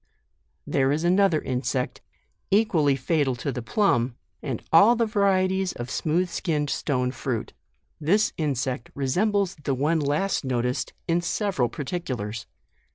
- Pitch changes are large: Yes, wide, 6.4 semitones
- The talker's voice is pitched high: No, medium, 150 Hz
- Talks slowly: Yes, slow, 130 wpm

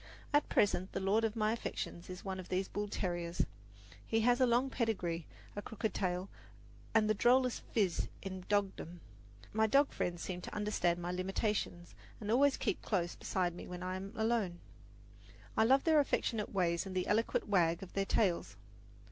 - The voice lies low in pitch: No, high, 195 Hz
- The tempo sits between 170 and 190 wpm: Yes, average, 180 wpm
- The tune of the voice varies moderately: Yes, average, 3.8 semitones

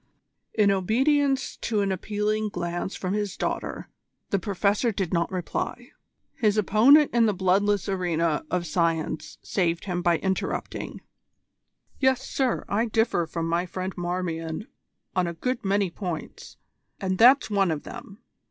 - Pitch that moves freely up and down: No, average, 3.6 semitones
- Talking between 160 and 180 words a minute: No, average, 145 wpm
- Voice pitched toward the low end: No, high, 195 Hz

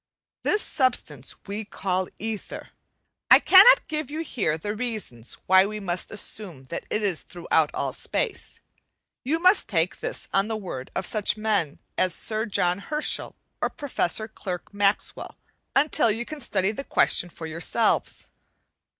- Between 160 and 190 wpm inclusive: No, average, 150 wpm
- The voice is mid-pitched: No, high, 210 Hz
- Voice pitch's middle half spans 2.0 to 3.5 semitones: No, average, 5.1 semitones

